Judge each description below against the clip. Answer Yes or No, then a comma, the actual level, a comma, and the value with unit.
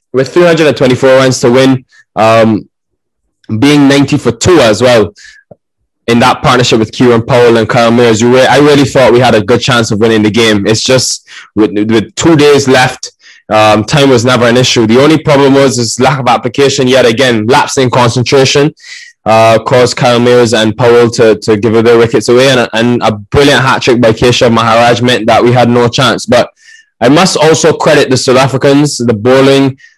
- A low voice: Yes, low, 125 Hz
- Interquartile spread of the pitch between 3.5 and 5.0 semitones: No, average, 2.7 semitones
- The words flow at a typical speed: Yes, average, 195 wpm